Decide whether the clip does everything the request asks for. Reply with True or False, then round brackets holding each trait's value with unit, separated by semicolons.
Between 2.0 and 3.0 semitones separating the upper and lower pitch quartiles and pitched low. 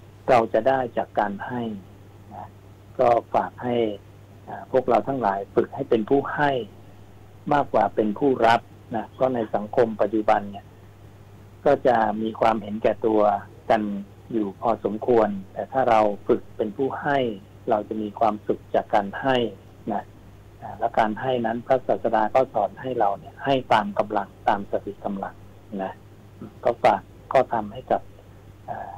True (2.5 semitones; 105 Hz)